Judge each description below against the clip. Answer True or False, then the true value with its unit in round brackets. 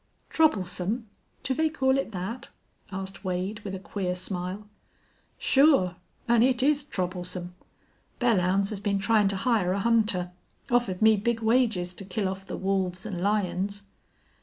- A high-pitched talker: True (200 Hz)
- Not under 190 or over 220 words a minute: False (150 wpm)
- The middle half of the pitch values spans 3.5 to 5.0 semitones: True (3.9 semitones)